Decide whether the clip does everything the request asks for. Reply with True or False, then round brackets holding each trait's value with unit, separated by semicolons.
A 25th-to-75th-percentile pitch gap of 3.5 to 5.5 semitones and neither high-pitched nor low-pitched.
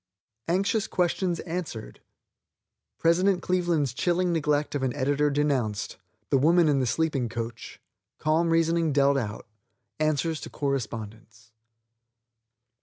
True (4.5 semitones; 150 Hz)